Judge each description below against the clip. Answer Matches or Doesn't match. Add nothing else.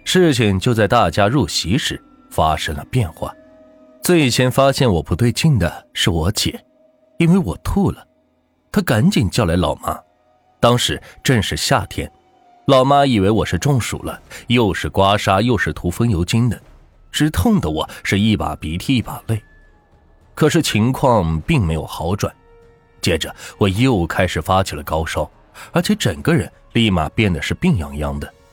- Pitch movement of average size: Doesn't match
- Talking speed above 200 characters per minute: Matches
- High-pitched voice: Doesn't match